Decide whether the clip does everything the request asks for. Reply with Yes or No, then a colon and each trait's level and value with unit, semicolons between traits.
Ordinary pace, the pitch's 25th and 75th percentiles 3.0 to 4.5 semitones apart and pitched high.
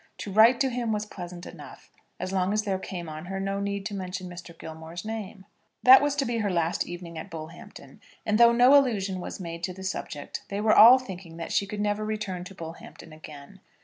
No: fast, 220 wpm; average, 3.6 semitones; high, 195 Hz